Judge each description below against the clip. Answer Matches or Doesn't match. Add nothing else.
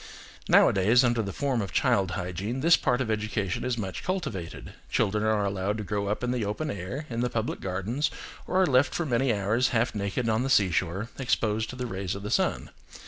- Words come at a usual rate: Doesn't match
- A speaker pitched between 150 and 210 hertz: Doesn't match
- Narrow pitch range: Doesn't match